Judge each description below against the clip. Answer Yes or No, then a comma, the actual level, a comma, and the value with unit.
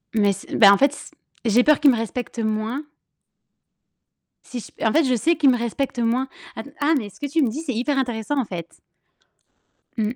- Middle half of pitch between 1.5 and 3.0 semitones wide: No, average, 4.1 semitones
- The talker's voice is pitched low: No, high, 245 Hz